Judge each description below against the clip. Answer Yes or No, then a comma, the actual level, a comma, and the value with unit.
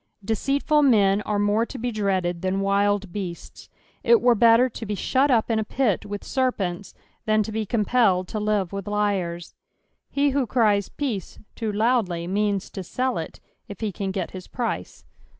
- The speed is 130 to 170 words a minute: No, average, 185 wpm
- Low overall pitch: No, high, 210 Hz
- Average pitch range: Yes, average, 3.3 semitones